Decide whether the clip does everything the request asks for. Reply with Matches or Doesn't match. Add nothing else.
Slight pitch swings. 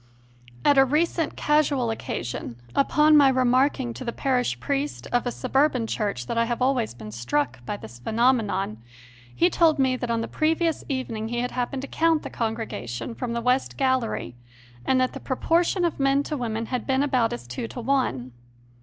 Doesn't match